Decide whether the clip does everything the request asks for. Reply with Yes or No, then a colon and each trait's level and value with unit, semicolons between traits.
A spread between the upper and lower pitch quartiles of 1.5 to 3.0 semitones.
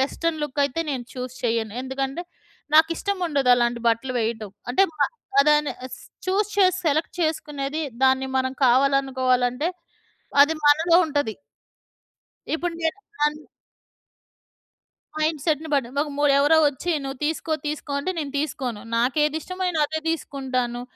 No: average, 3.6 semitones